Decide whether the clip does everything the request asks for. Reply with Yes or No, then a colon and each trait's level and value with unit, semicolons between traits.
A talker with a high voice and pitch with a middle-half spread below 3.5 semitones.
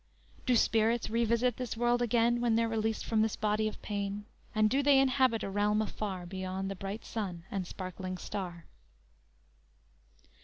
Yes: high, 215 Hz; average, 3.1 semitones